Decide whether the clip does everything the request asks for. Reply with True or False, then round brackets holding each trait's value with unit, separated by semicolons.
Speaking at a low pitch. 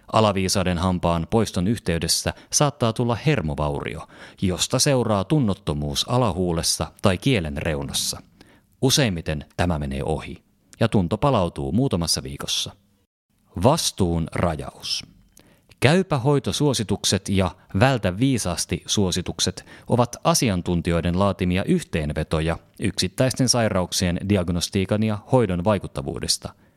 True (95 Hz)